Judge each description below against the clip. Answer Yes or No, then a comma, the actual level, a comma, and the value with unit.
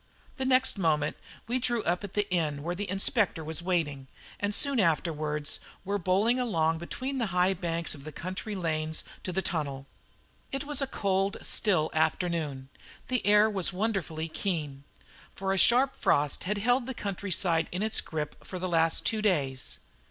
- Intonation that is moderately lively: Yes, average, 4.8 semitones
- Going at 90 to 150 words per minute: No, average, 175 wpm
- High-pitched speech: No, medium, 180 Hz